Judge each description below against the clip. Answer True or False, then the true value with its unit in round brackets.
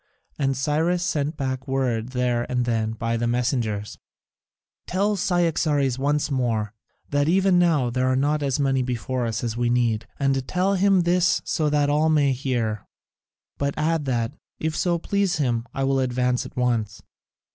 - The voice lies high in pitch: False (135 Hz)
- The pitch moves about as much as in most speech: True (4.1 semitones)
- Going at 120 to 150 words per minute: False (170 wpm)